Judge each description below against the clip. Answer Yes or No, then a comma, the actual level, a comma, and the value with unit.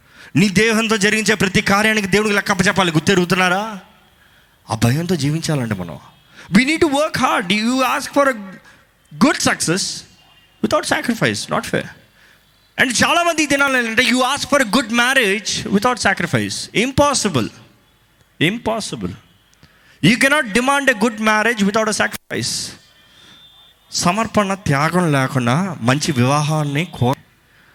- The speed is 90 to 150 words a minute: Yes, average, 120 wpm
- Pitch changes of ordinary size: No, wide, 6.9 semitones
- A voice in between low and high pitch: No, high, 205 Hz